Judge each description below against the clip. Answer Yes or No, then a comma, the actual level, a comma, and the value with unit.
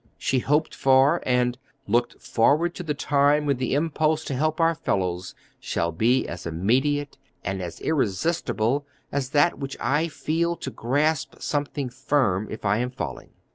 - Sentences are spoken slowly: No, average, 160 wpm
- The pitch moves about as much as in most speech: Yes, average, 4.5 semitones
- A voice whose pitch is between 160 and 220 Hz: No, low, 135 Hz